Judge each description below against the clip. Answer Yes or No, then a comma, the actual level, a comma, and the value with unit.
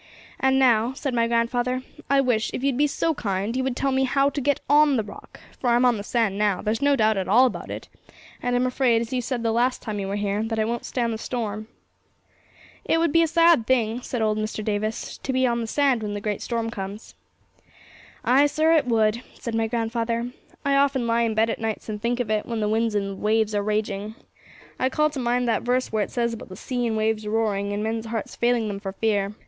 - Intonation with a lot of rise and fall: No, average, 2.9 semitones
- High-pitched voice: Yes, high, 230 Hz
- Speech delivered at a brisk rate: Yes, fast, 250 wpm